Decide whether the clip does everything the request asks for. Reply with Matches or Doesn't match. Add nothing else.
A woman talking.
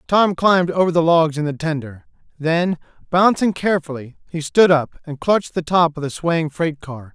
Doesn't match